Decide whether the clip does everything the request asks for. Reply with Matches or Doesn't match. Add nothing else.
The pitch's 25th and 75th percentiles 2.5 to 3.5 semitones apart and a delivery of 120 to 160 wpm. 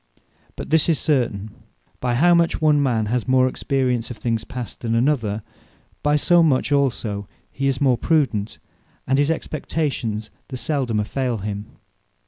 Doesn't match